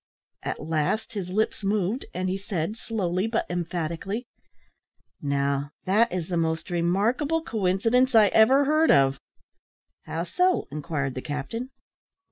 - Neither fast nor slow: No, slow, 130 wpm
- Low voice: No, medium, 185 Hz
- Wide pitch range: Yes, wide, 5.7 semitones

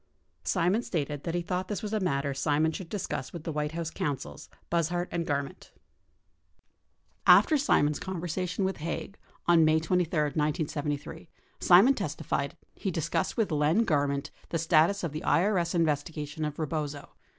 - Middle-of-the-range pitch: Yes, medium, 165 Hz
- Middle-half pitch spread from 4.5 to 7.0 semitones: No, average, 3.3 semitones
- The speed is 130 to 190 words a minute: Yes, average, 160 wpm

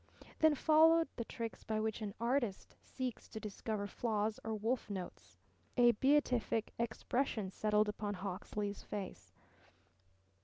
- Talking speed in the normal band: No, slow, 125 wpm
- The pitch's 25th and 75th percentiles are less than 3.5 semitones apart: Yes, average, 3.0 semitones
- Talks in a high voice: Yes, high, 220 Hz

